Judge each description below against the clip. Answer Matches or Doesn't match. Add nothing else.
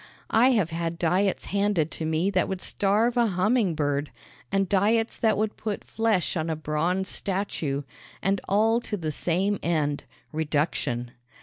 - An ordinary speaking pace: Matches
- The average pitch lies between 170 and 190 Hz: Matches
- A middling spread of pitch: Matches